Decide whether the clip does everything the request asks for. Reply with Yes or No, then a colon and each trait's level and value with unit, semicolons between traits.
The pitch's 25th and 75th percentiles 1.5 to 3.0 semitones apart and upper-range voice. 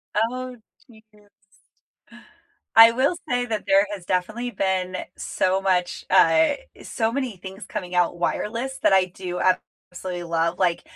No: average, 4.0 semitones; high, 195 Hz